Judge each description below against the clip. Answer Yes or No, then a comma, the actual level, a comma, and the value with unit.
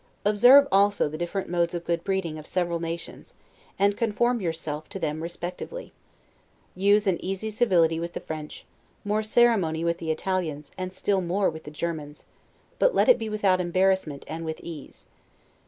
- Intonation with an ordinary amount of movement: Yes, average, 3.8 semitones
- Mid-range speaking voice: Yes, medium, 175 Hz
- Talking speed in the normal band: Yes, average, 170 wpm